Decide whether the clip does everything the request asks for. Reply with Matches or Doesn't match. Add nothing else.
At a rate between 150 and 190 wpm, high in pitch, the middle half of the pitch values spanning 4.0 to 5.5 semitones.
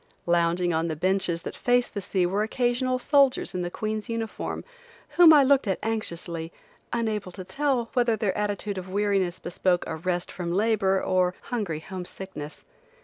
Matches